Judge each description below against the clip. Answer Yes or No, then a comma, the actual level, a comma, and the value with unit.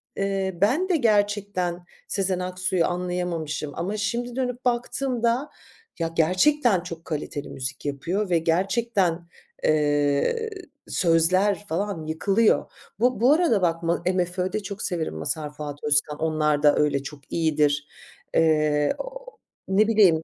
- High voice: No, medium, 180 Hz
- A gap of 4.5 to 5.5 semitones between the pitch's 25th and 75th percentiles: Yes, average, 4.9 semitones